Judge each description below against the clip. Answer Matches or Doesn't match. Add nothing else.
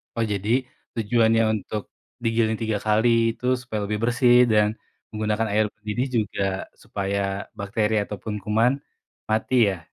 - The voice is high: Doesn't match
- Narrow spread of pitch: Matches